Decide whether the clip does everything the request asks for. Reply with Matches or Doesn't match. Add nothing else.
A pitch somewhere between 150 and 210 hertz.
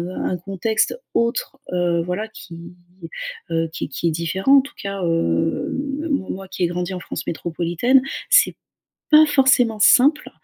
Matches